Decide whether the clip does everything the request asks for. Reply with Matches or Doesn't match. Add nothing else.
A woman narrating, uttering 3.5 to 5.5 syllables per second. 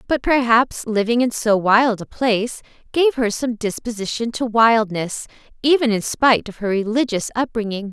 Matches